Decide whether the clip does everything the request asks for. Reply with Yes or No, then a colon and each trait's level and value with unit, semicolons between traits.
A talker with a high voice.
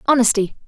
Yes: high, 235 Hz